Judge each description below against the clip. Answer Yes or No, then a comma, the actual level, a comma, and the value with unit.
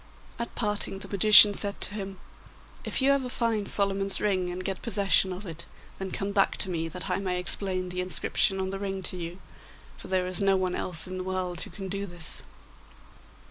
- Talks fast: Yes, fast, 210 wpm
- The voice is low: No, high, 190 Hz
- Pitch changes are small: Yes, narrow, 1.7 semitones